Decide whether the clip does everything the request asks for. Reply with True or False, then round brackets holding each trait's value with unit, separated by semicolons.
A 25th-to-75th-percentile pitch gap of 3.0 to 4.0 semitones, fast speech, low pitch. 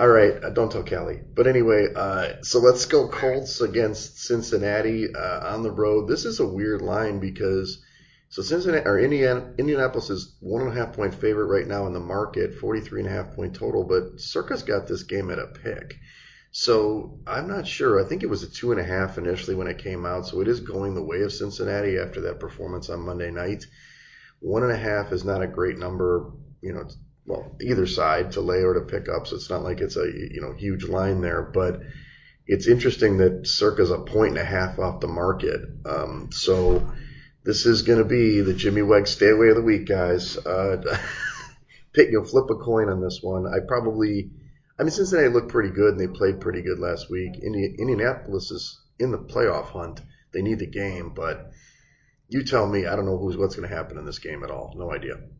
False (4.6 semitones; 220 wpm; 105 Hz)